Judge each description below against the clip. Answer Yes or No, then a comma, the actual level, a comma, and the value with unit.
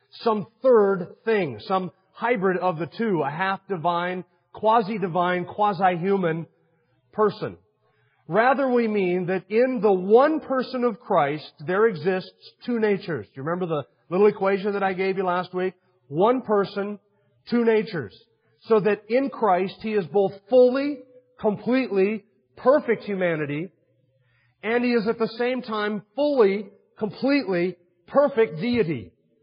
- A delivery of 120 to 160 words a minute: Yes, slow, 135 wpm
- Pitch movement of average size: Yes, average, 4.3 semitones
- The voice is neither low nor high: No, high, 195 Hz